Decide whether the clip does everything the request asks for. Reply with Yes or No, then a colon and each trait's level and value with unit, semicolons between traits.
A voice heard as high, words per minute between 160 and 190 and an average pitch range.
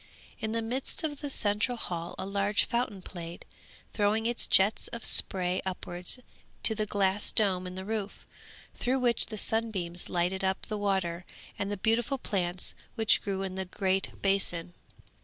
Yes: high, 200 Hz; average, 165 wpm; average, 3.2 semitones